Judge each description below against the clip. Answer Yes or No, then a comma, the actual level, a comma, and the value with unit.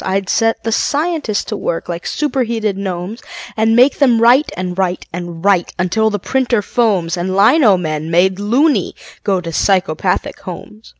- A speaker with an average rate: Yes, average, 165 wpm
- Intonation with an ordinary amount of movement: Yes, average, 4.4 semitones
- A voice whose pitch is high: Yes, high, 200 Hz